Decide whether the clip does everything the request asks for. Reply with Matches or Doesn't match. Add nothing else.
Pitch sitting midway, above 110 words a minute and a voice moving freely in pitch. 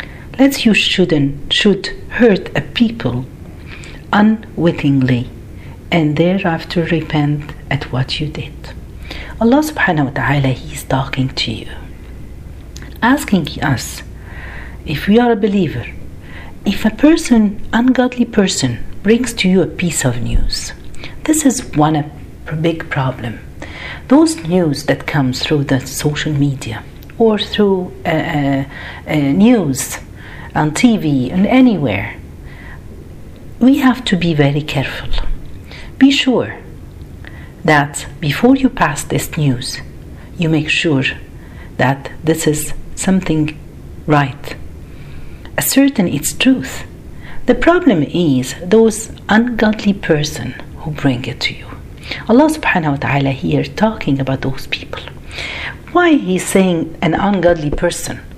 Matches